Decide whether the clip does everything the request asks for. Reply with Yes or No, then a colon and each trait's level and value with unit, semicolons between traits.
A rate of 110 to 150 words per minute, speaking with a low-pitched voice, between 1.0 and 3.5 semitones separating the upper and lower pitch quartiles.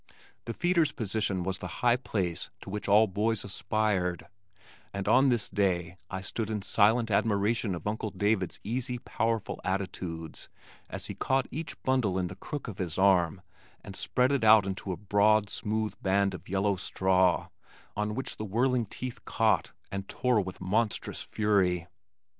No: average, 165 wpm; low, 105 Hz; average, 3.0 semitones